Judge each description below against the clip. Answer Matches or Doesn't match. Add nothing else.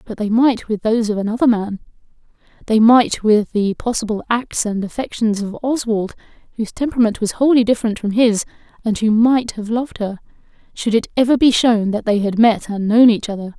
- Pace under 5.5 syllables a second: Doesn't match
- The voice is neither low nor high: Doesn't match